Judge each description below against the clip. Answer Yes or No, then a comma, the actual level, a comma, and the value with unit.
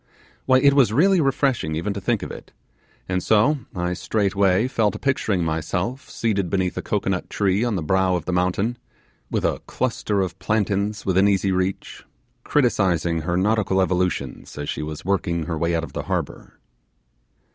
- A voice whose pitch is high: No, very low, 95 Hz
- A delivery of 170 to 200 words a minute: Yes, average, 175 wpm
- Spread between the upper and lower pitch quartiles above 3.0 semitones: Yes, average, 3.8 semitones